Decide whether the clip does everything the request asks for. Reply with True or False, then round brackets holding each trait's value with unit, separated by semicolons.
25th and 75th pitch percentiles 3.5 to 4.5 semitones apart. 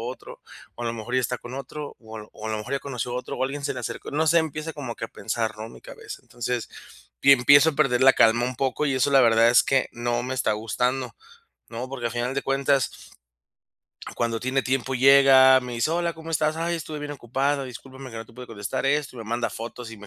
False (2.8 semitones)